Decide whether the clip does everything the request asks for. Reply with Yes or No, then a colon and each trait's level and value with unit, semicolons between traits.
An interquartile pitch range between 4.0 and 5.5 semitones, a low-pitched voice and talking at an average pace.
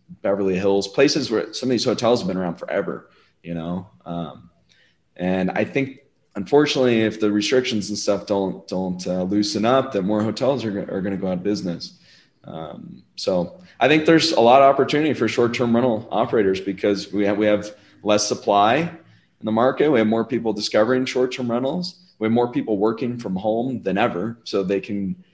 Yes: average, 4.5 semitones; low, 105 Hz; average, 195 wpm